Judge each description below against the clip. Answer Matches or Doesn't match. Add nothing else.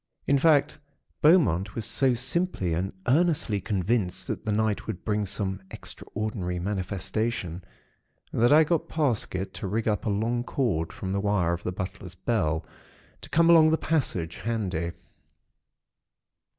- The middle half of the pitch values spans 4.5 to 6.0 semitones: Matches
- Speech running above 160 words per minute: Doesn't match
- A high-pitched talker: Doesn't match